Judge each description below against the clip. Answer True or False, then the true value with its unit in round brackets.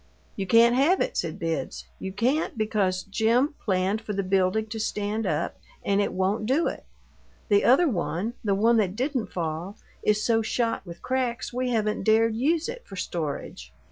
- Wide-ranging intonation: False (3.8 semitones)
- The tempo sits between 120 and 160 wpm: False (180 wpm)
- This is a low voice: False (215 Hz)